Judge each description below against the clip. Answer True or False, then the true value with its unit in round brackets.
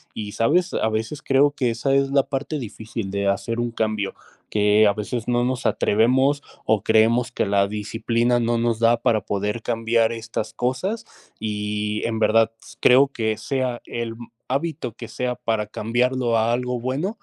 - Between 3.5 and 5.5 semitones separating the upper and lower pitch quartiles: False (2.6 semitones)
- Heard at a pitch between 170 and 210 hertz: False (115 Hz)